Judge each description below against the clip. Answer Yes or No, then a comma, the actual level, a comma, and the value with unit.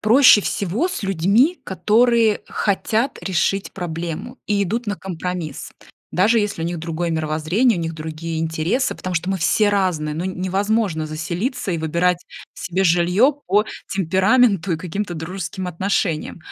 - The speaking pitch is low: No, medium, 185 Hz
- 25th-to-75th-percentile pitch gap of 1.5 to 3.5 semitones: No, average, 3.9 semitones